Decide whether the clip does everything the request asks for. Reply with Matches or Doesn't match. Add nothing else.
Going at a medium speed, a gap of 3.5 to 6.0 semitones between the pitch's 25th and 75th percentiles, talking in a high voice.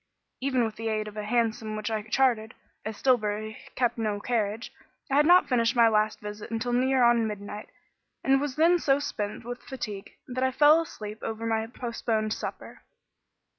Doesn't match